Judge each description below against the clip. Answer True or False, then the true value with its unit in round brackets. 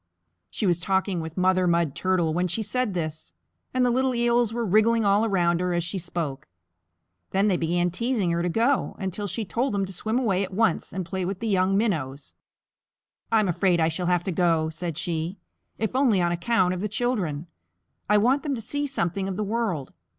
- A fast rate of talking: True (210 wpm)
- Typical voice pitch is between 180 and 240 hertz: True (190 Hz)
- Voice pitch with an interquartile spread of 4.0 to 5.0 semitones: True (4.4 semitones)